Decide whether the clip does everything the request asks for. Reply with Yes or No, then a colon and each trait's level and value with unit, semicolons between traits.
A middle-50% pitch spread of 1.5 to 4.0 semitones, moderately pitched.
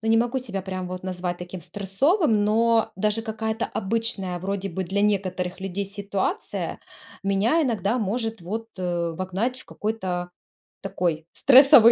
No: average, 3.5 semitones; high, 200 Hz